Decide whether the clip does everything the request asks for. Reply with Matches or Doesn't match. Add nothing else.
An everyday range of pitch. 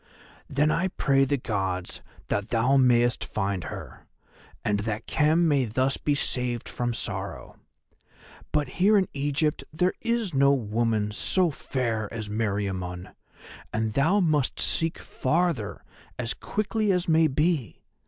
Doesn't match